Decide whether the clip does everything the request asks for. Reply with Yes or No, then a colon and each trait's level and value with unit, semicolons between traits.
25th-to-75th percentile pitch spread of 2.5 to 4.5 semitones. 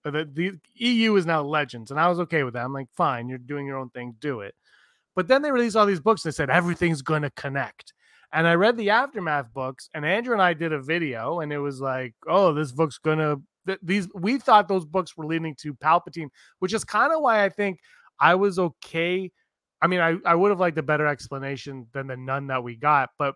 No: average, 5.0 semitones